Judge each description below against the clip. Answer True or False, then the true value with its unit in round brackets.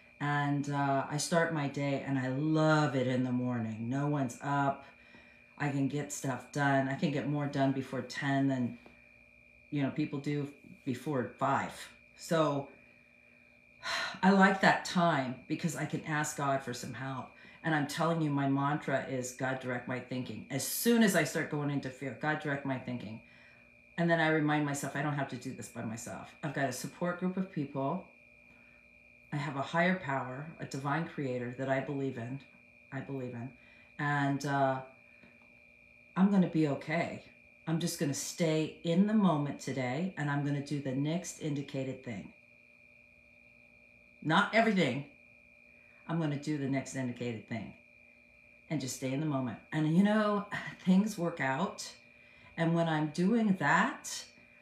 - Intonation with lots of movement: False (3.5 semitones)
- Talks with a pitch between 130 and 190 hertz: True (140 Hz)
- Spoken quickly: False (170 wpm)